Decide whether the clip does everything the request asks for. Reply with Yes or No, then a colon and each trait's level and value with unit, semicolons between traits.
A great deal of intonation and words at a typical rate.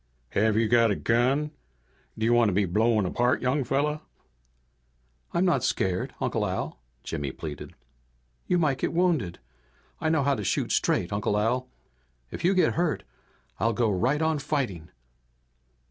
Yes: wide, 6.2 semitones; average, 160 wpm